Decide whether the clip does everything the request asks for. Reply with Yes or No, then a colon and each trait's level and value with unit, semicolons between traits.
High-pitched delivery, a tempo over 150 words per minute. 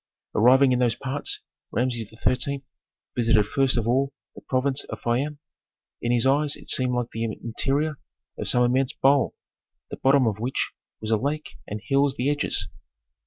No: low, 130 Hz; average, 165 wpm